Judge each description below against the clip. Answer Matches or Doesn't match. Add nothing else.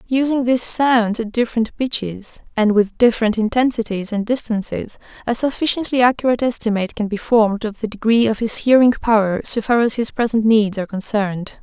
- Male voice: Doesn't match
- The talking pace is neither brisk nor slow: Matches